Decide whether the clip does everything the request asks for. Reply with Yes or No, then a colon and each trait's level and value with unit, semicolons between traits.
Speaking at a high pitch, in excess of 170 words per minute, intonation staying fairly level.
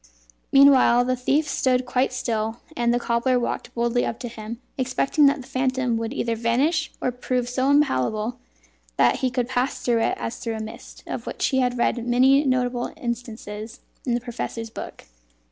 Yes: high, 245 Hz; average, 180 wpm; narrow, 1.8 semitones